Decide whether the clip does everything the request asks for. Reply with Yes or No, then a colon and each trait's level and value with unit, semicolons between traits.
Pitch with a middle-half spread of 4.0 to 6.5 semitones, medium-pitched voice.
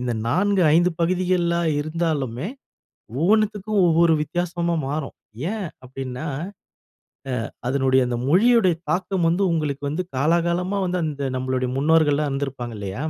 Yes: average, 4.8 semitones; medium, 160 Hz